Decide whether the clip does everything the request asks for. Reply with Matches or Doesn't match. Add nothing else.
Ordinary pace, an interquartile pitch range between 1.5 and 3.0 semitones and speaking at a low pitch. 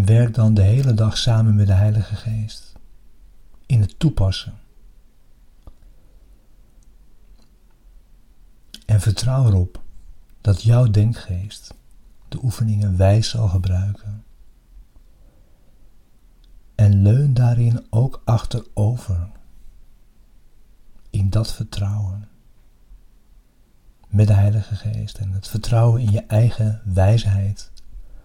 Doesn't match